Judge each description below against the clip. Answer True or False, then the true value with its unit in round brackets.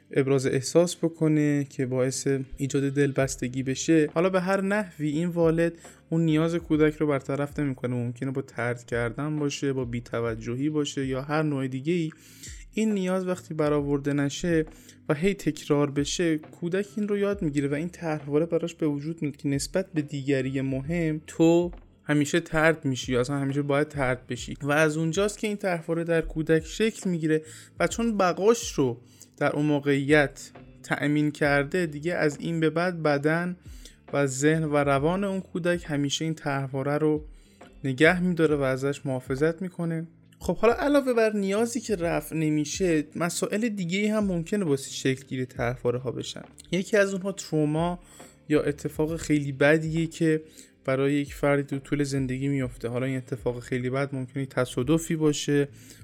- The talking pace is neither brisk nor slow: False (165 wpm)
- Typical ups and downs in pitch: True (3.5 semitones)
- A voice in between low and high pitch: True (150 Hz)